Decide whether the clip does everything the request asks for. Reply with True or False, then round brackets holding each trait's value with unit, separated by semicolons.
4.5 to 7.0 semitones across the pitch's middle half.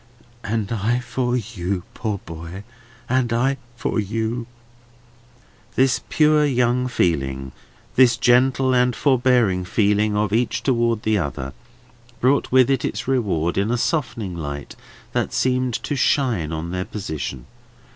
True (5.3 semitones)